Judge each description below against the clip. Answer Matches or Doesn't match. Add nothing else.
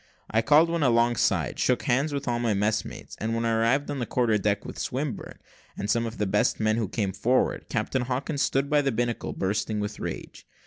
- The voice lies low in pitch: Matches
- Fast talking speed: Matches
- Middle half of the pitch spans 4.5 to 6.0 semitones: Doesn't match